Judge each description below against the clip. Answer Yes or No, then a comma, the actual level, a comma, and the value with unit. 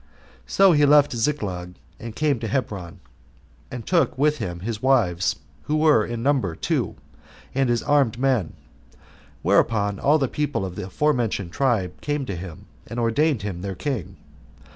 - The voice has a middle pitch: No, low, 115 Hz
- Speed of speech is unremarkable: Yes, average, 160 wpm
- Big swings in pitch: Yes, wide, 6.8 semitones